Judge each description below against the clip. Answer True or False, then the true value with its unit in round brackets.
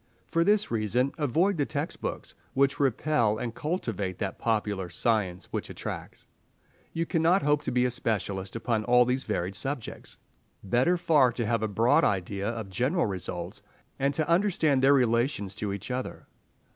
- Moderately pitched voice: False (120 Hz)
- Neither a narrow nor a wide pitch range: False (5.9 semitones)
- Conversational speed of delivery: True (165 wpm)